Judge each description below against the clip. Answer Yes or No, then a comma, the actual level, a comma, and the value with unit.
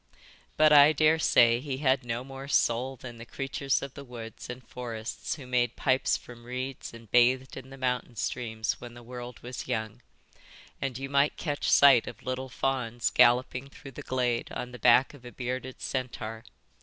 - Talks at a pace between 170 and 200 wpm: Yes, average, 180 wpm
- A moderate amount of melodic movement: No, narrow, 2.0 semitones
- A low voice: Yes, low, 125 Hz